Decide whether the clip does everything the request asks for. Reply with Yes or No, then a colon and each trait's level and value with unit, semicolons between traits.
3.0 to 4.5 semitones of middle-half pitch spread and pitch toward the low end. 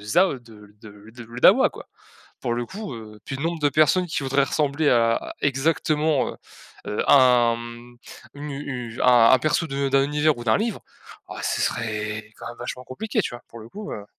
Yes: average, 4.2 semitones; low, 125 Hz